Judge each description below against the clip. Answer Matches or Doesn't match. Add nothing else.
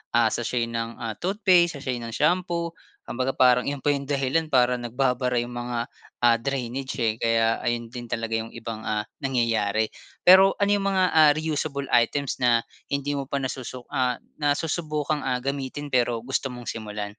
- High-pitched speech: Doesn't match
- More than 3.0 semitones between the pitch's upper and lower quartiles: Matches